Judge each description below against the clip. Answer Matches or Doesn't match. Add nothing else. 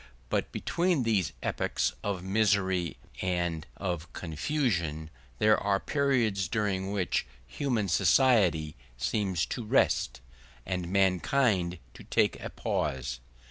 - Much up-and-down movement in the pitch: Doesn't match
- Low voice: Matches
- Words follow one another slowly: Matches